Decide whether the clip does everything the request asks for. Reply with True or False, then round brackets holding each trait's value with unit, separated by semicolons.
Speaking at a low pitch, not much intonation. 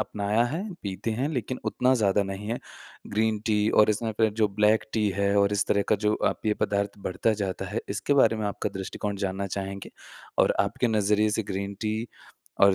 True (105 Hz; 1.8 semitones)